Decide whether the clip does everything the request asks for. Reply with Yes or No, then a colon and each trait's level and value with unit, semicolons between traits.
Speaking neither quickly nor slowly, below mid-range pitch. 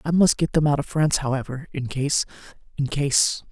No: average, 190 wpm; medium, 145 Hz